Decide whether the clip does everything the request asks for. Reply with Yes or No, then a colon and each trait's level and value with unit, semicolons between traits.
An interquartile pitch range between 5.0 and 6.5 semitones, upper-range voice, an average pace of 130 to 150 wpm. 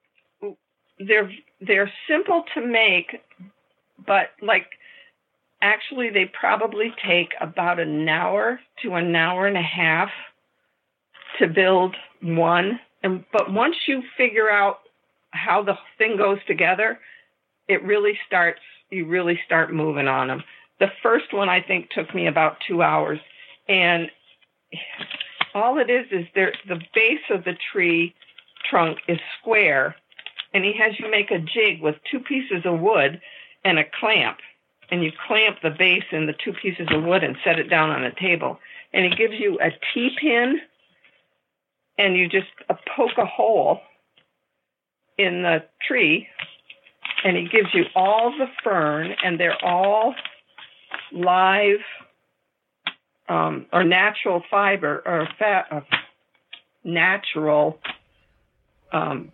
No: average, 4.6 semitones; high, 195 Hz; average, 140 wpm